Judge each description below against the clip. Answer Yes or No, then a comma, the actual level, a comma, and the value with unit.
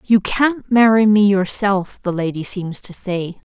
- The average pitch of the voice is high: Yes, high, 200 Hz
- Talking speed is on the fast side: No, average, 170 wpm